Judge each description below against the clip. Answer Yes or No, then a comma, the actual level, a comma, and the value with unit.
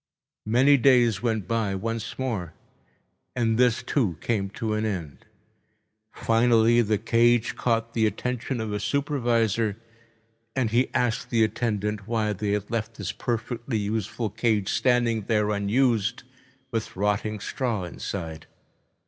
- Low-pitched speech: Yes, low, 115 Hz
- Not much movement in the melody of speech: Yes, narrow, 2.3 semitones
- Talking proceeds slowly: Yes, slow, 130 wpm